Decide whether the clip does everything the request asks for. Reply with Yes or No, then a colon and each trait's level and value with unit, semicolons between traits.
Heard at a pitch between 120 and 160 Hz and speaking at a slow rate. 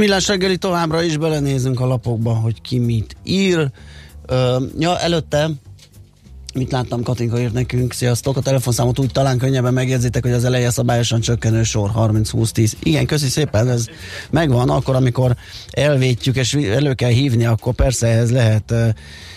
No: low, 125 Hz; fast, 155 wpm